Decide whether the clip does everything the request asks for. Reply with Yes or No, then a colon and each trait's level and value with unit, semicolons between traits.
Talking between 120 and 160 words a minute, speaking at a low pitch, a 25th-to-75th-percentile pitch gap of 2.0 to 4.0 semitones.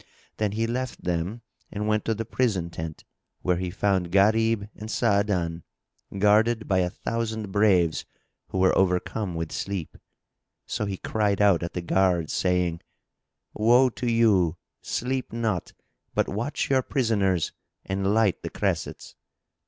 Yes: average, 145 wpm; low, 100 Hz; average, 3.7 semitones